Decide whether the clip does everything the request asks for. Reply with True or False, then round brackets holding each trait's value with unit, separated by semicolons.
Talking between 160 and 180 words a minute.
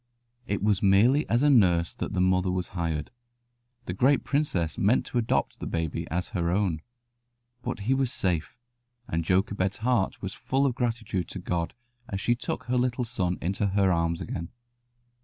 True (175 wpm)